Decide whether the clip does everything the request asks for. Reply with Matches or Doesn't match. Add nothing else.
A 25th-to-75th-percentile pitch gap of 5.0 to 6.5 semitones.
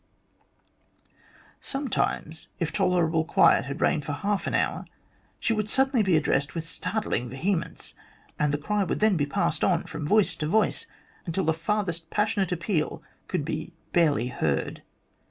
Matches